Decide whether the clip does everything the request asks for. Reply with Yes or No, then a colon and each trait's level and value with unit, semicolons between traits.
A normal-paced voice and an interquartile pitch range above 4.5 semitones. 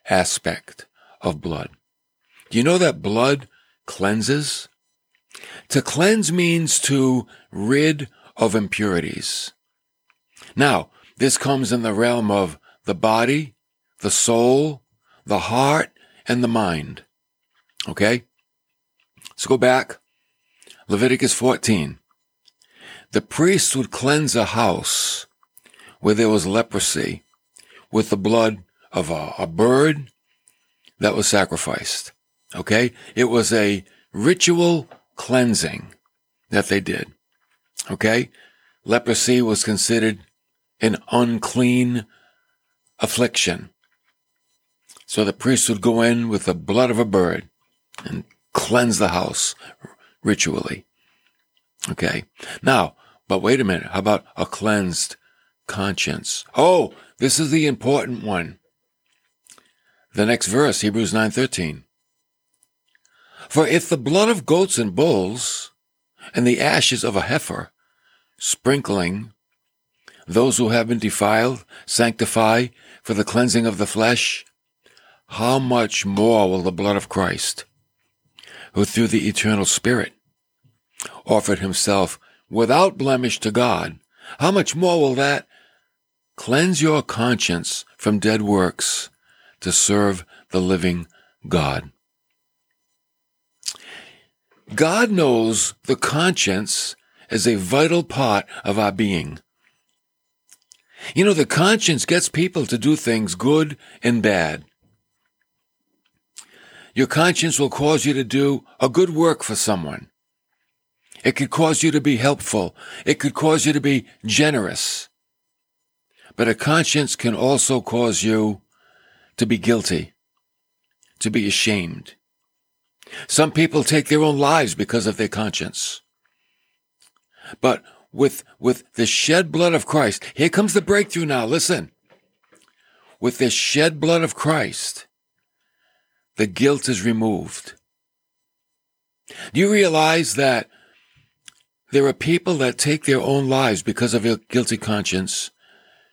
No: slow, 120 wpm; wide, 5.4 semitones